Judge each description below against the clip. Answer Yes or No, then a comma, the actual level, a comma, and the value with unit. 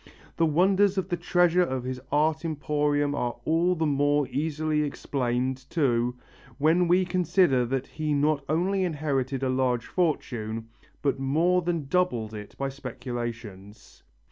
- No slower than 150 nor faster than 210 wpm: No, average, 140 wpm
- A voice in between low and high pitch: Yes, medium, 145 Hz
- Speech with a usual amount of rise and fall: Yes, average, 4.7 semitones